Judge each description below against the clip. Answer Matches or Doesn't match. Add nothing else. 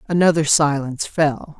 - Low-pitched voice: Doesn't match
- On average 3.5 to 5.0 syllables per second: Matches